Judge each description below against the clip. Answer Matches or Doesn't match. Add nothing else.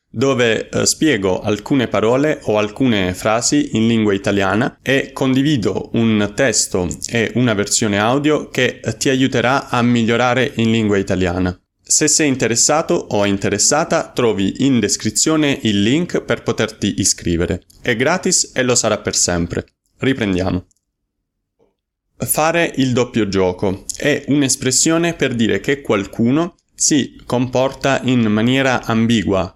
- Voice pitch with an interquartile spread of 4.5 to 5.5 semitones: Matches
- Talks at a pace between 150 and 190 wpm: Doesn't match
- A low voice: Matches